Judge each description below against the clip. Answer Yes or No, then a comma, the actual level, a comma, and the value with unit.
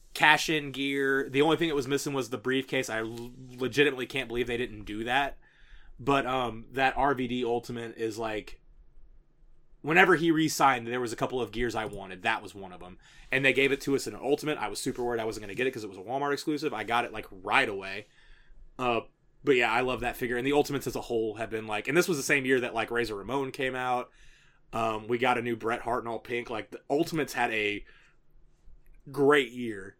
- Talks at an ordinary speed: No, fast, 240 wpm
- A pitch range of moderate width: Yes, average, 3.2 semitones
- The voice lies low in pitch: Yes, low, 125 Hz